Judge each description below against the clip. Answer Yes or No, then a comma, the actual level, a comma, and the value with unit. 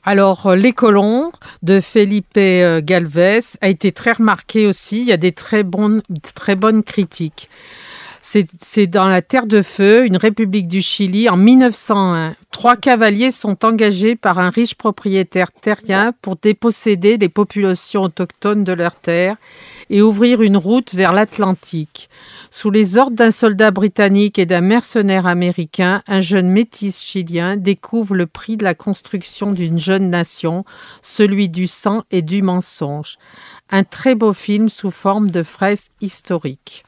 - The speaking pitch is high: Yes, high, 200 Hz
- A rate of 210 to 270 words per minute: No, average, 155 wpm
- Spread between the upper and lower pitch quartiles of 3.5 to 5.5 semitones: No, average, 2.9 semitones